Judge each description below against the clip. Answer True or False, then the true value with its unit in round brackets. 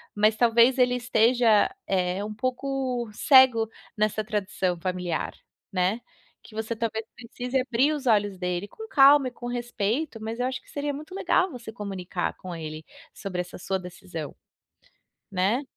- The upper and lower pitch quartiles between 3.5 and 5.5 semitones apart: True (4.8 semitones)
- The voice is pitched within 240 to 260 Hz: False (225 Hz)